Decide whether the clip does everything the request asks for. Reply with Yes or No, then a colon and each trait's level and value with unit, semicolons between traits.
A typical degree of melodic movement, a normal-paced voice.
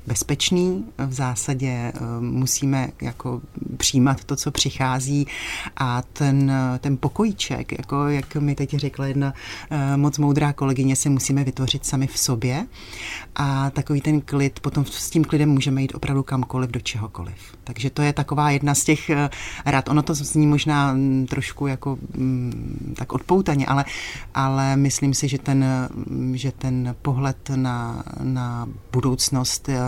No: narrow, 1.9 semitones; average, 140 wpm